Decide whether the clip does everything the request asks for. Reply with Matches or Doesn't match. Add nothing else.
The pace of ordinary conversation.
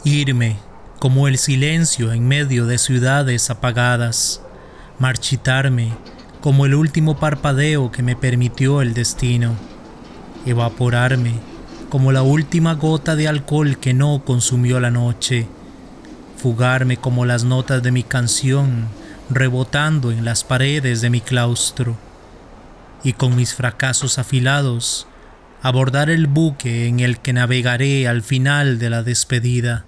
Doesn't match